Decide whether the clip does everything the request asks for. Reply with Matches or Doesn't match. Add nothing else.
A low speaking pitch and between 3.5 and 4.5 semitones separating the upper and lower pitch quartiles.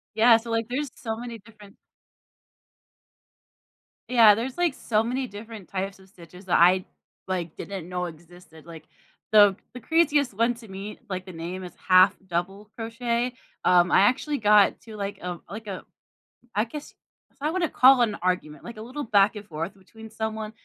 Doesn't match